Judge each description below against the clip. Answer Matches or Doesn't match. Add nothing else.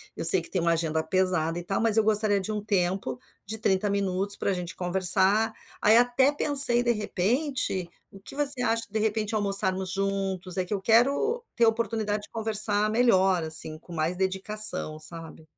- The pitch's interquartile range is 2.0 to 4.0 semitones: Matches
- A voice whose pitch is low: Doesn't match